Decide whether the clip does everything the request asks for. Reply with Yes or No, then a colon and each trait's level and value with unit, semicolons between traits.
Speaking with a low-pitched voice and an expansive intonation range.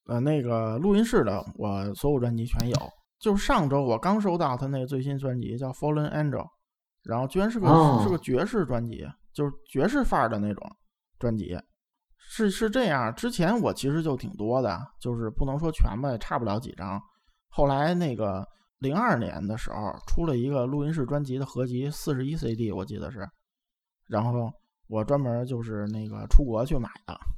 Yes: low, 130 Hz; wide, 6.0 semitones